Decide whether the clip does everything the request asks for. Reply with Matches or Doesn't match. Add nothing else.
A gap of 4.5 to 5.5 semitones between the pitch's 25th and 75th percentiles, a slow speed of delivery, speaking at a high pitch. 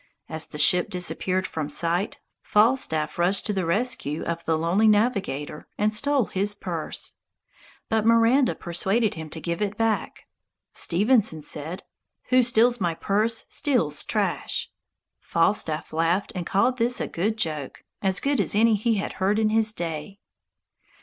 Doesn't match